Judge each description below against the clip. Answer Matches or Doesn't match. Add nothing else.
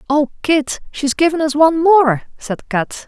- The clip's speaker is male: Doesn't match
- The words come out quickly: Doesn't match